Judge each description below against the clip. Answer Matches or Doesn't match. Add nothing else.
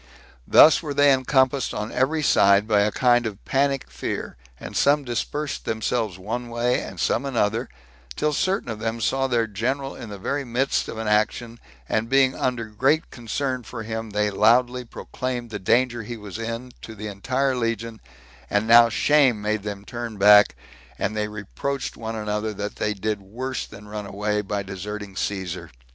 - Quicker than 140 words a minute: Matches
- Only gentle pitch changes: Doesn't match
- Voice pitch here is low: Matches